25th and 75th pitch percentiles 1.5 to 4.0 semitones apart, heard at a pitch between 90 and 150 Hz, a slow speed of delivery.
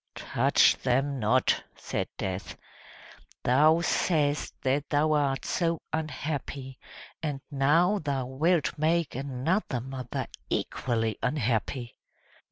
Yes: average, 3.3 semitones; medium, 140 Hz; slow, 100 wpm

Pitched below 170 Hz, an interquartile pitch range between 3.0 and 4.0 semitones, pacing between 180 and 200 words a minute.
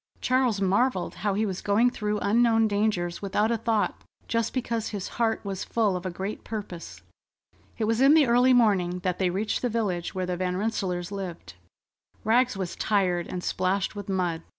No: high, 205 Hz; average, 3.6 semitones; average, 185 wpm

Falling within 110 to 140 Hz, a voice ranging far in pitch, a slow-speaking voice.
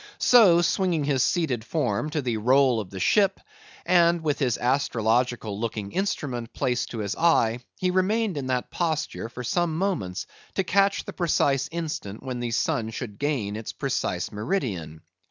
No: low, 135 Hz; wide, 6.9 semitones; average, 165 wpm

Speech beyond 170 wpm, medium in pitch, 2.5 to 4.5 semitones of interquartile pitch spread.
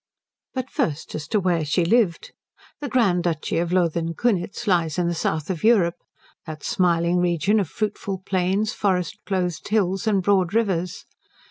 No: average, 160 wpm; medium, 180 Hz; average, 3.2 semitones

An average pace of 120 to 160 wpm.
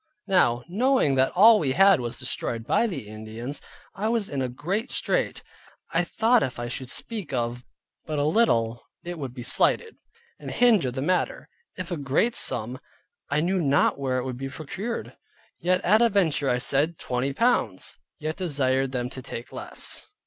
No: average, 185 wpm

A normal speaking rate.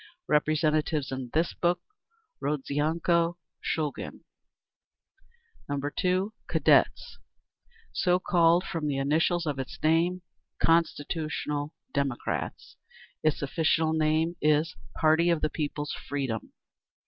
No: slow, 95 wpm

